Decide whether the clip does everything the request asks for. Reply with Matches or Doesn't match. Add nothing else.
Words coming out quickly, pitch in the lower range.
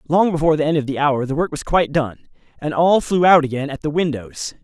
Doesn't match